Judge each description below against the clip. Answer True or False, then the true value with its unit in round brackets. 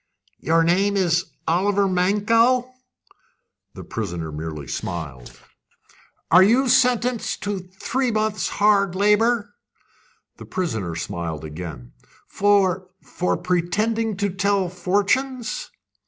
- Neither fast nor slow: False (100 wpm)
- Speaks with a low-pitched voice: False (195 Hz)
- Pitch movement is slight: False (4.5 semitones)